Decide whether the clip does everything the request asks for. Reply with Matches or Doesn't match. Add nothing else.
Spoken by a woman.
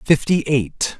Doesn't match